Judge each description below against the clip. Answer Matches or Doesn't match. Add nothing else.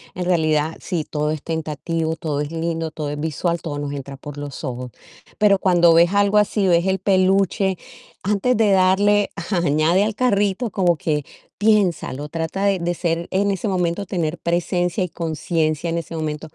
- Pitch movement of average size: Matches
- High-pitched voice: Doesn't match